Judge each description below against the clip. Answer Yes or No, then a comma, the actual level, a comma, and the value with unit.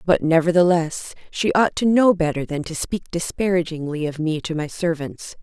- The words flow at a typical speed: Yes, average, 175 wpm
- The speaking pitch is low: No, medium, 170 Hz